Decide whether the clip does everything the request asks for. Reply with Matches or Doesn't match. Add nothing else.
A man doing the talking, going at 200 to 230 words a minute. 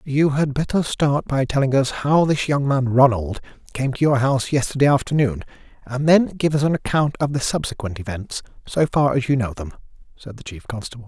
Matches